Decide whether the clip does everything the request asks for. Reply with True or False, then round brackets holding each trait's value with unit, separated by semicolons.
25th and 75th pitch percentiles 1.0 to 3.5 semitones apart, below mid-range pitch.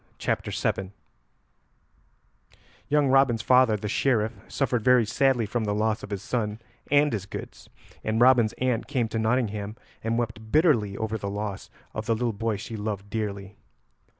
True (2.9 semitones; 110 Hz)